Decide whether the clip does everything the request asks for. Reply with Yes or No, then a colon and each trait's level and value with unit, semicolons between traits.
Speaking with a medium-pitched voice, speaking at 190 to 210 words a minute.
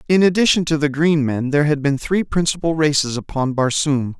Yes: medium, 150 Hz; average, 200 wpm